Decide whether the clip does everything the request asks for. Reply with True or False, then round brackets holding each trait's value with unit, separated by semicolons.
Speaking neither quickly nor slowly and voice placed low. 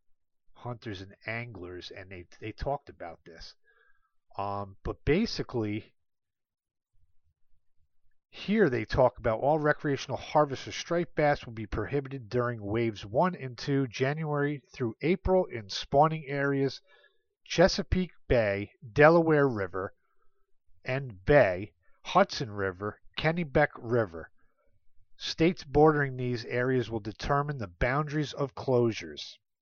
False (115 wpm; 130 Hz)